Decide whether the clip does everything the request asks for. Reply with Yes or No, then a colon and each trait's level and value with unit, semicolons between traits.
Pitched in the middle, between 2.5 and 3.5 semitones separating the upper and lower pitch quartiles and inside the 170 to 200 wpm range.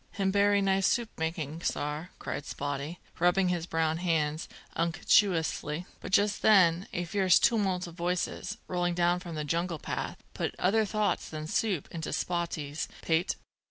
No: medium, 175 Hz; average, 3.1 semitones; average, 155 wpm